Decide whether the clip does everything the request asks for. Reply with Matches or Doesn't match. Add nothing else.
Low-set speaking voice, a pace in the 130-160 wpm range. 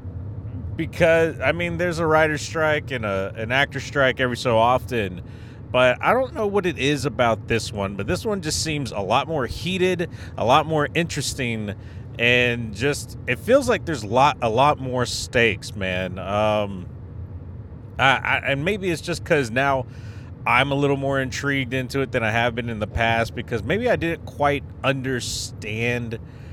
Doesn't match